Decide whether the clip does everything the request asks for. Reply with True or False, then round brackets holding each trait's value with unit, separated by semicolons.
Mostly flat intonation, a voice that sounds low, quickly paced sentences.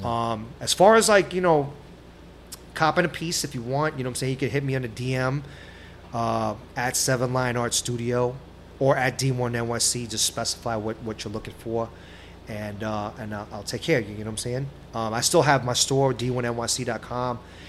False (3.4 semitones; 120 Hz; 210 wpm)